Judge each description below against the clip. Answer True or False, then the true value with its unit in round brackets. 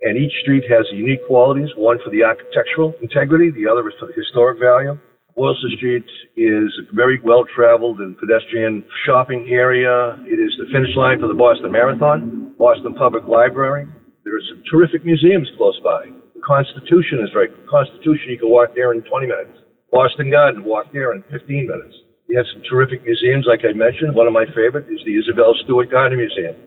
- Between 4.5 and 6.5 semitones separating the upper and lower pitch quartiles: True (4.8 semitones)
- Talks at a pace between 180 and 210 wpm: True (195 wpm)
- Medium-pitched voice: False (130 Hz)